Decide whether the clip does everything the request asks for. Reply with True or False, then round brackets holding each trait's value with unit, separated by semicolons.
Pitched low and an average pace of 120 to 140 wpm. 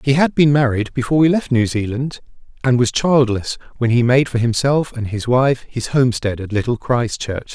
False (125 Hz; 200 wpm)